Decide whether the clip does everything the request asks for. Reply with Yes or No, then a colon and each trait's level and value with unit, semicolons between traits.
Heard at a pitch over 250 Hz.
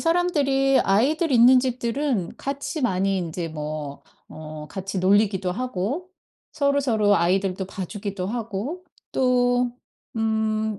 No: high, 220 Hz